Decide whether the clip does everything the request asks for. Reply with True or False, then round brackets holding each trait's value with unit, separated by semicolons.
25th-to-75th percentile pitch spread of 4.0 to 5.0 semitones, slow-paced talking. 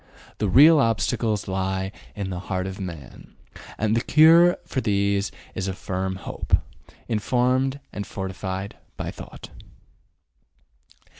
True (4.3 semitones; 125 wpm)